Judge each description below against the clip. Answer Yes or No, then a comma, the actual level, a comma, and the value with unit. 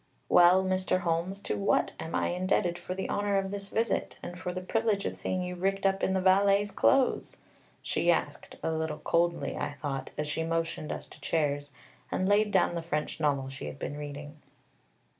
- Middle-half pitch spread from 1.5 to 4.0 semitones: Yes, average, 3.6 semitones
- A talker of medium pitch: Yes, medium, 180 Hz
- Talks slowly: No, average, 195 wpm